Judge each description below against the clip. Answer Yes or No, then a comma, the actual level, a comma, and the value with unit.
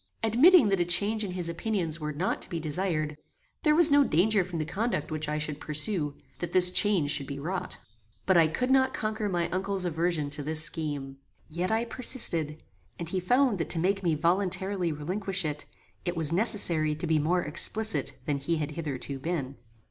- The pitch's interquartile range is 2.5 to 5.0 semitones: Yes, average, 4.5 semitones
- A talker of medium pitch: Yes, medium, 170 Hz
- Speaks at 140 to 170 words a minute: No, average, 195 wpm